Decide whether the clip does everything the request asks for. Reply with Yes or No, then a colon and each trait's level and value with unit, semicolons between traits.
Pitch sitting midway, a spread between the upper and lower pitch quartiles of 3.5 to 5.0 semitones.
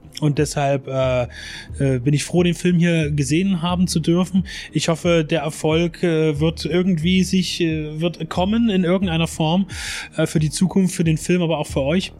No: medium, 165 Hz; narrow, 2.5 semitones